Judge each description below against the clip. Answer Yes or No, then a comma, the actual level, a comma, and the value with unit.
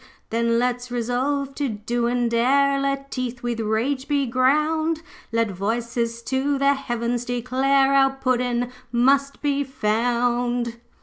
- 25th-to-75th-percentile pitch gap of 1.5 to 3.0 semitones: Yes, average, 2.7 semitones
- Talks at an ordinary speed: No, slow, 130 wpm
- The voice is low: No, high, 245 Hz